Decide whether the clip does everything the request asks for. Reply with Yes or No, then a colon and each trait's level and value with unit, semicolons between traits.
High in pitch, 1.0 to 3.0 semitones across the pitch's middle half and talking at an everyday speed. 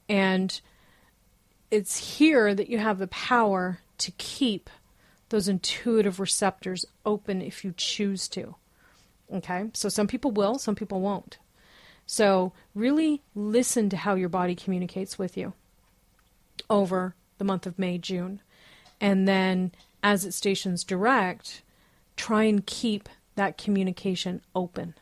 No: high, 195 Hz; narrow, 2.4 semitones; slow, 130 wpm